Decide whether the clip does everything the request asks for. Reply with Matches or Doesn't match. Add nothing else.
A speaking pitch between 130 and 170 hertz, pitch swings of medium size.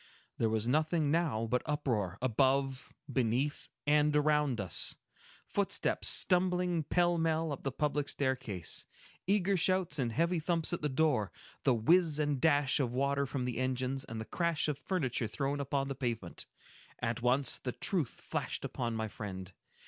Matches